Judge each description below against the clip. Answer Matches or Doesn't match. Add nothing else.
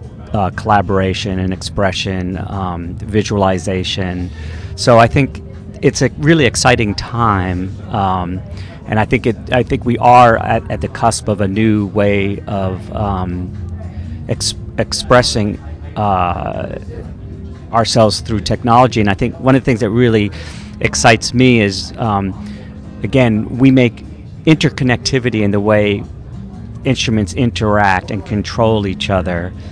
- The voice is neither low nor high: Doesn't match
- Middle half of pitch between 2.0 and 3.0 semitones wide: Doesn't match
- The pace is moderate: Doesn't match